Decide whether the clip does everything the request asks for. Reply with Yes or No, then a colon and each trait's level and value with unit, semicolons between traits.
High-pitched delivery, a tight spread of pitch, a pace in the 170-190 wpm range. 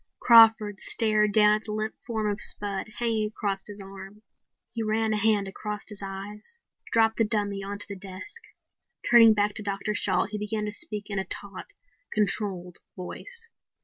Yes: high, 210 Hz; narrow, 1.6 semitones; average, 175 wpm